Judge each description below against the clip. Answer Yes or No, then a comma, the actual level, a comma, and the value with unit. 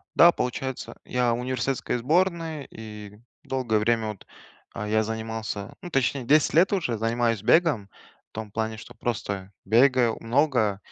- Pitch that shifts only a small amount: No, average, 3.7 semitones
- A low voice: Yes, low, 115 Hz